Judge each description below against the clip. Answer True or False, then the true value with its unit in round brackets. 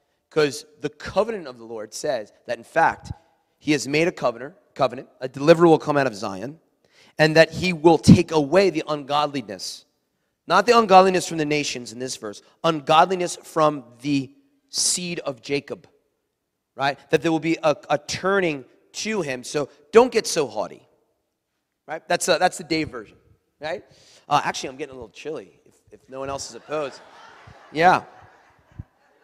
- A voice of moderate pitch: True (155 Hz)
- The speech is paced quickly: False (170 wpm)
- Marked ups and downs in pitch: False (3.9 semitones)